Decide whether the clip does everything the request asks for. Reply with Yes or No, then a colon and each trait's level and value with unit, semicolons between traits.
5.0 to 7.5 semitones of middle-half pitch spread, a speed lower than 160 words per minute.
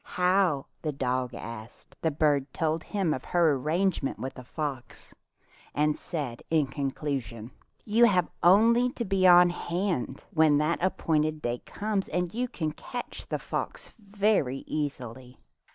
Yes: wide, 5.5 semitones; average, 150 wpm